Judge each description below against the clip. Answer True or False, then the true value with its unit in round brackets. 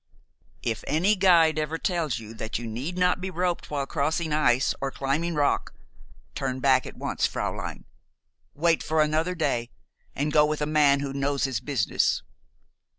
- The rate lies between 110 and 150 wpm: False (165 wpm)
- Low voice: False (150 Hz)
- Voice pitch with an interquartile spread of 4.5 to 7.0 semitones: False (3.2 semitones)